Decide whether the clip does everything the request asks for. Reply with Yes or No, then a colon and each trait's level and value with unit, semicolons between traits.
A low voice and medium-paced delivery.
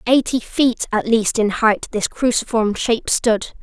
No: high, 230 Hz; average, 165 wpm